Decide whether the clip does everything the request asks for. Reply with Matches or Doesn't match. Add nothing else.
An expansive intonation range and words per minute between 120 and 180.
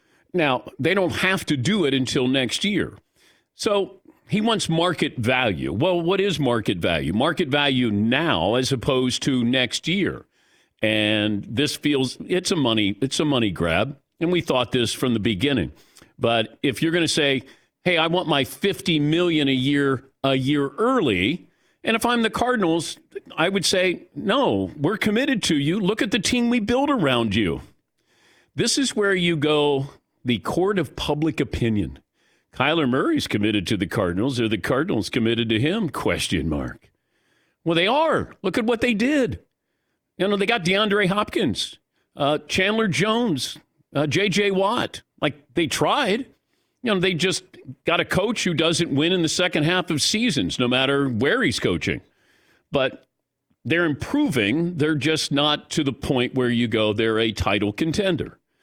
Matches